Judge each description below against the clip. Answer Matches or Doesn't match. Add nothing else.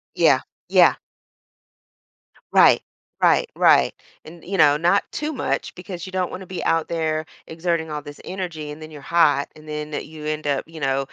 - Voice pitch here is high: Doesn't match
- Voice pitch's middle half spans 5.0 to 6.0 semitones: Doesn't match